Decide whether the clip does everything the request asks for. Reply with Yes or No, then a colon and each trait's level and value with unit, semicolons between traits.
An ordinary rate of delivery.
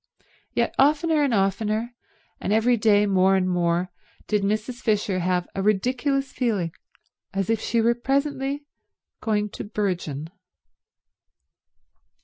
No: slow, 125 wpm